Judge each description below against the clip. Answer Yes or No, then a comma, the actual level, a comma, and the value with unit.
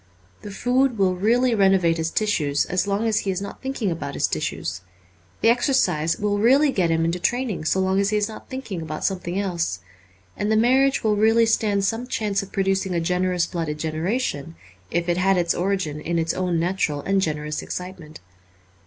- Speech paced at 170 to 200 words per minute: Yes, average, 195 wpm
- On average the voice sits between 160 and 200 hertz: Yes, high, 190 Hz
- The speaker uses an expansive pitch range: No, average, 4.5 semitones